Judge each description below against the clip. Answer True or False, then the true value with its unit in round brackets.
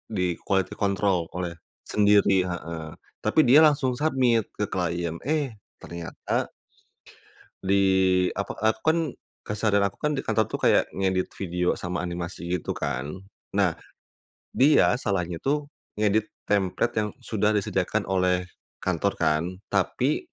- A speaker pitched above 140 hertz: False (100 Hz)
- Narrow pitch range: False (3.5 semitones)